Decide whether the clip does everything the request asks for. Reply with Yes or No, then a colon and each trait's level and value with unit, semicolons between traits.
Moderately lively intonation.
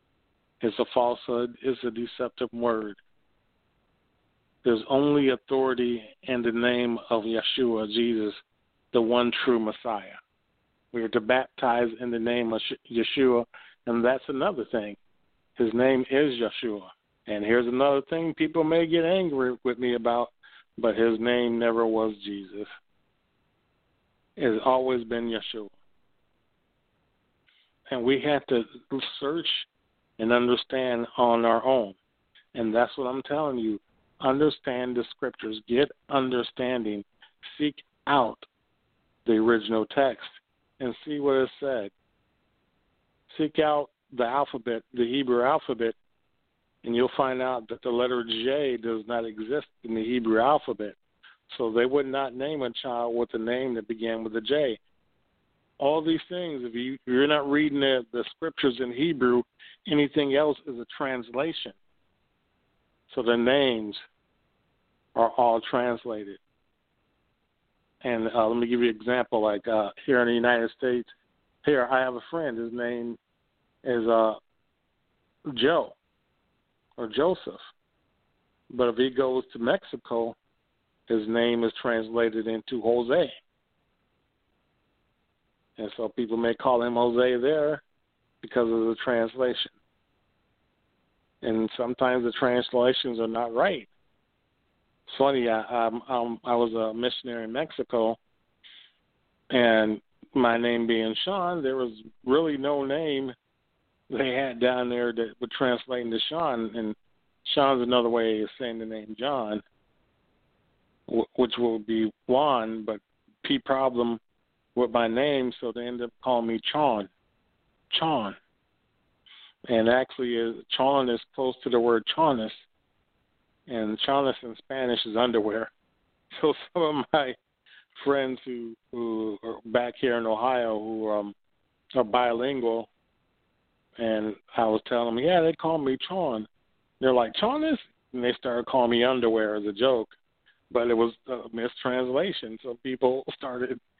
No: narrow, 2.3 semitones